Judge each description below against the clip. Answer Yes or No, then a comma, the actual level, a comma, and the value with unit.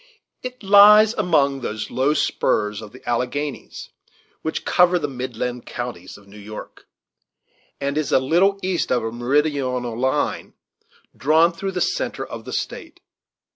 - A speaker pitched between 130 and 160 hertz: Yes, medium, 140 Hz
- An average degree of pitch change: No, wide, 6.1 semitones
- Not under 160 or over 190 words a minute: No, average, 150 wpm